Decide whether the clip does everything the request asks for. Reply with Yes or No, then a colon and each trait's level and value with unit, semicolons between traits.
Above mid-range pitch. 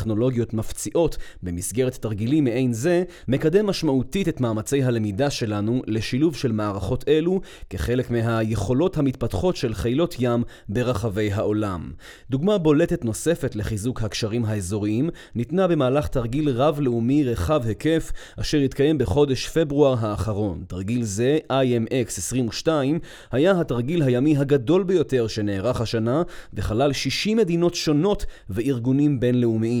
No: low, 125 Hz